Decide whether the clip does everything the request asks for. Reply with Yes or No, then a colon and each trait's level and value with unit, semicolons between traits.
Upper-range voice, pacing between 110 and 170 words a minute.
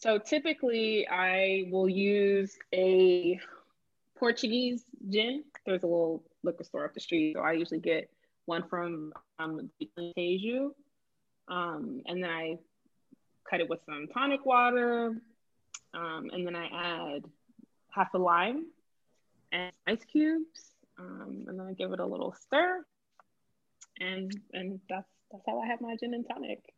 Yes: high, 195 Hz; average, 145 wpm